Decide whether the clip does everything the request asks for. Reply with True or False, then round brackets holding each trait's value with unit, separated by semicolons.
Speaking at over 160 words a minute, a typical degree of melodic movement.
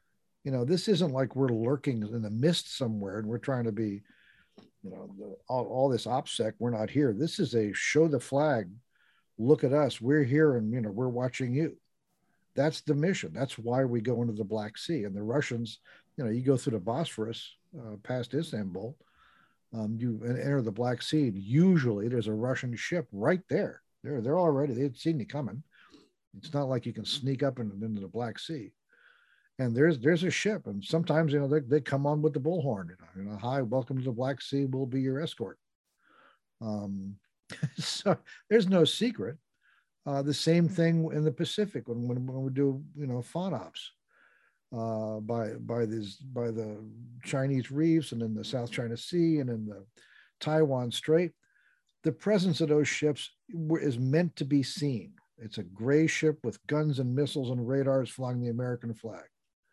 True (195 wpm; 4.9 semitones)